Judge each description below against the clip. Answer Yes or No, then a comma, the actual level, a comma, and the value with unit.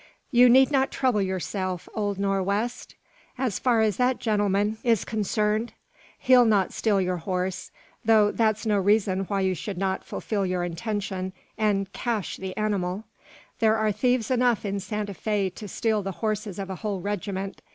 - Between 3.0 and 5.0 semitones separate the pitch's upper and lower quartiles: No, narrow, 2.5 semitones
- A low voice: No, high, 205 Hz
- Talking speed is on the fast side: No, average, 170 wpm